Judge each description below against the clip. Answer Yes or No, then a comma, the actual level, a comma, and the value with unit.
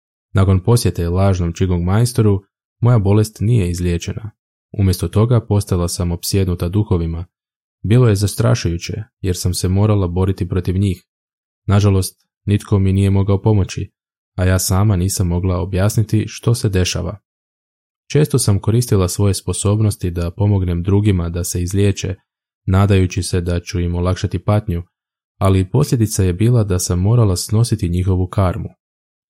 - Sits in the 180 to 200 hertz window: No, very low, 95 Hz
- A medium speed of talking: Yes, average, 140 wpm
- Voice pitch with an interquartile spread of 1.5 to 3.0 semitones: Yes, average, 2.7 semitones